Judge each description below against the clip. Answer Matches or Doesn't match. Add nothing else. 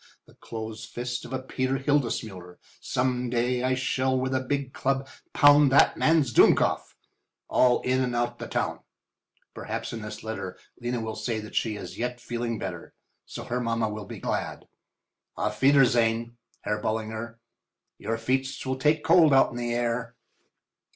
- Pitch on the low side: Matches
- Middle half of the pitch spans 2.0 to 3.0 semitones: Matches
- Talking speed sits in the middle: Matches